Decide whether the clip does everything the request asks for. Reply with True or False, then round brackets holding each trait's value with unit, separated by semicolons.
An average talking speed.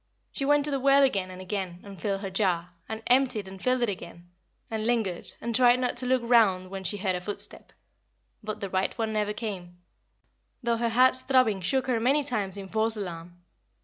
False (210 wpm)